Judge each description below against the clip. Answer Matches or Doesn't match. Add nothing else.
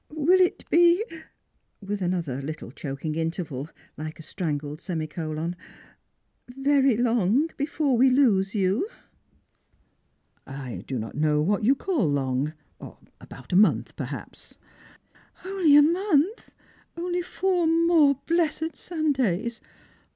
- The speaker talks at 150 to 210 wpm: Doesn't match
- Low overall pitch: Doesn't match